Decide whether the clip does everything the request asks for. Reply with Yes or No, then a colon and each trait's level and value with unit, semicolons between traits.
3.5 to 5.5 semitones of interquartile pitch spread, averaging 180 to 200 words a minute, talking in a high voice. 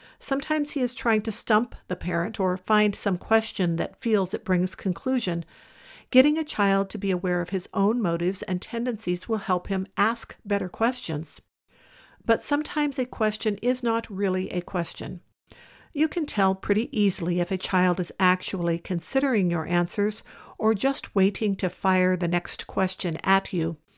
No: average, 3.9 semitones; average, 170 wpm; high, 195 Hz